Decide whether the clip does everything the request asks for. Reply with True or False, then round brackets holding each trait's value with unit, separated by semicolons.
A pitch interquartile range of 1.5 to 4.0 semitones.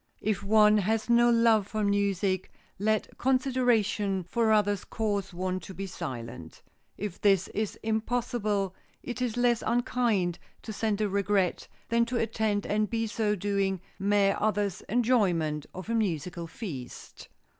True (2.8 semitones)